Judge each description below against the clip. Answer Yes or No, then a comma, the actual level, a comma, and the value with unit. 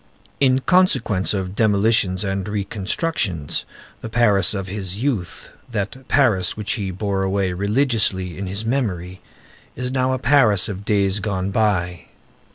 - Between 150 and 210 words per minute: No, average, 140 wpm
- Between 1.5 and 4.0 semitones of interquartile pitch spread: Yes, average, 3.5 semitones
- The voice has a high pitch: No, low, 100 Hz